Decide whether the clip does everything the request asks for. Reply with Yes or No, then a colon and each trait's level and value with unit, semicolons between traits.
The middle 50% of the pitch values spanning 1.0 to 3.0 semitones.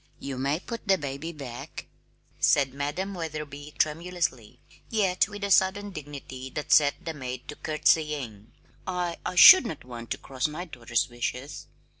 No: average, 5.2 semitones